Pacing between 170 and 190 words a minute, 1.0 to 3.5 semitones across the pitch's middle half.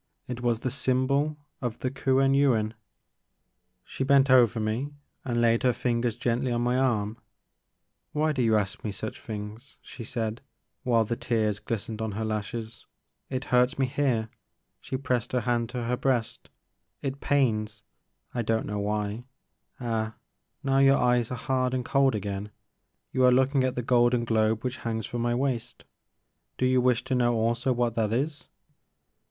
Yes: average, 180 wpm; average, 2.7 semitones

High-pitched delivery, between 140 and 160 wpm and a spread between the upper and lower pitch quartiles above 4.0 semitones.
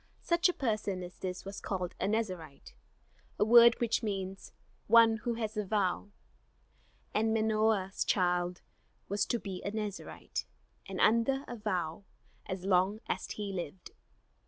No: high, 205 Hz; average, 145 wpm; average, 3.0 semitones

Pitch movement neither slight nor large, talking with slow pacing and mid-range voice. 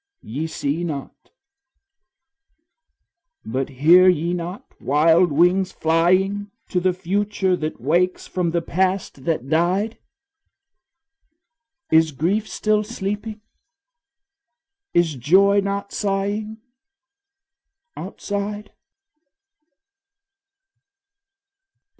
Yes: average, 3.7 semitones; slow, 80 wpm; medium, 180 Hz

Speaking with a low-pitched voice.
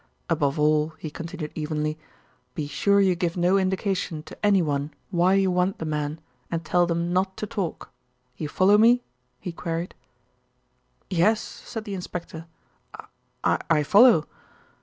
No: medium, 175 Hz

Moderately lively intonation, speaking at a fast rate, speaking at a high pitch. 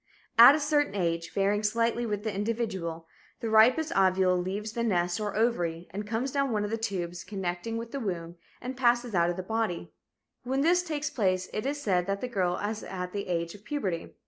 Yes: average, 4.5 semitones; fast, 210 wpm; high, 210 Hz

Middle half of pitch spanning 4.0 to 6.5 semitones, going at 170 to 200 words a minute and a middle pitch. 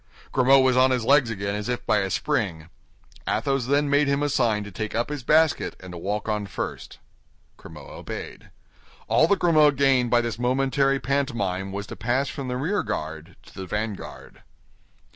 No: average, 5.2 semitones; average, 185 wpm; low, 125 Hz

